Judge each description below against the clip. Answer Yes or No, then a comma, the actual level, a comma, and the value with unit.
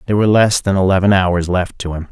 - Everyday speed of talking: No, fast, 255 wpm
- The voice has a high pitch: No, very low, 95 Hz